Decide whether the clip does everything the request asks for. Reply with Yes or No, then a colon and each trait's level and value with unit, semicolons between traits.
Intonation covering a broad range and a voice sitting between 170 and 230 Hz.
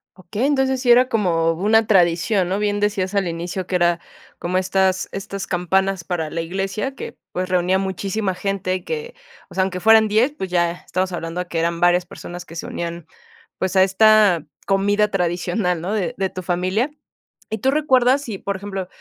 No: average, 2.9 semitones; high, 190 Hz